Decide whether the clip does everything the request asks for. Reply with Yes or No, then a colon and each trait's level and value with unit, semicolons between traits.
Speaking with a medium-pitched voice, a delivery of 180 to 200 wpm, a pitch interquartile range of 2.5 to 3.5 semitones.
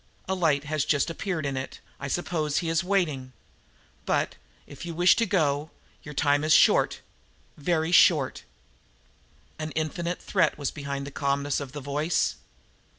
No: medium, 155 Hz; average, 155 wpm; average, 3.2 semitones